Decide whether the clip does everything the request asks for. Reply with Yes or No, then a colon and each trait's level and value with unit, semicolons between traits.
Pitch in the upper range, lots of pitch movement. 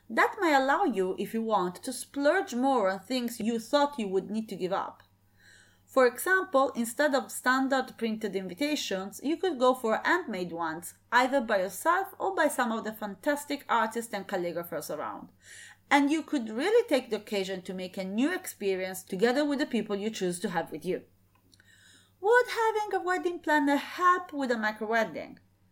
Yes: high, 230 Hz; wide, 7.1 semitones